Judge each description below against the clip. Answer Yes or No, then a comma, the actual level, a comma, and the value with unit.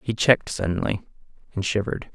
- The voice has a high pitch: No, low, 105 Hz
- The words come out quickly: No, average, 140 wpm